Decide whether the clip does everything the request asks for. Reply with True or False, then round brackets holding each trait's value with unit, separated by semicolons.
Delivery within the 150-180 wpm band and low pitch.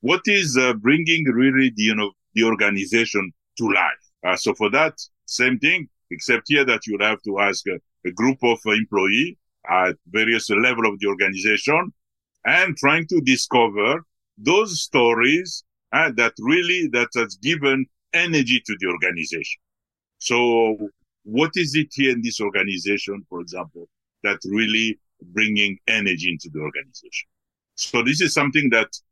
True (155 wpm; 115 Hz)